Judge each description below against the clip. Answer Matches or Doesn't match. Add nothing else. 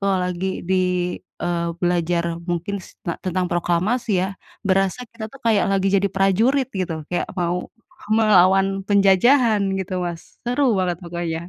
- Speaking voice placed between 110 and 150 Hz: Doesn't match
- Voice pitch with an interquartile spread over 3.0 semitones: Doesn't match